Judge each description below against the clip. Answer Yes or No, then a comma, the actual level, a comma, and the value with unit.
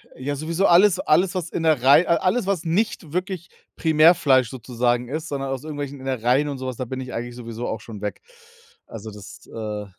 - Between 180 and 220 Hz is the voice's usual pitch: No, low, 135 Hz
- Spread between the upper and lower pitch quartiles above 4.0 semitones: Yes, wide, 5.5 semitones